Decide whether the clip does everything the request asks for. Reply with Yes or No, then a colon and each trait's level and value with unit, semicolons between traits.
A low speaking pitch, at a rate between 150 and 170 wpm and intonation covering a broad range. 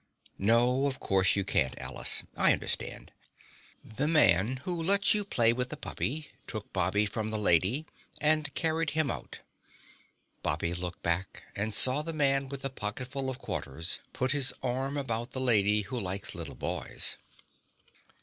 Yes: low, 125 Hz; average, 160 wpm; wide, 5.9 semitones